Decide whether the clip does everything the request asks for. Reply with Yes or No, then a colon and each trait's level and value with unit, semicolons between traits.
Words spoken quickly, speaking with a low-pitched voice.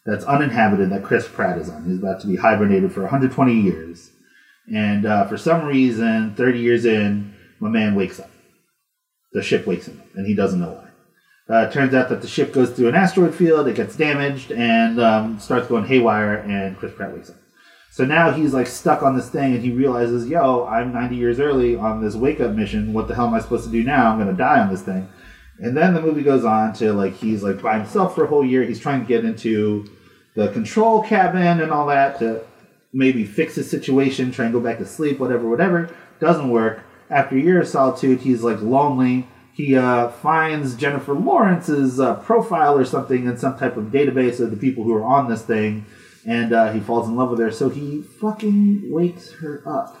Yes: fast, 220 wpm; low, 125 Hz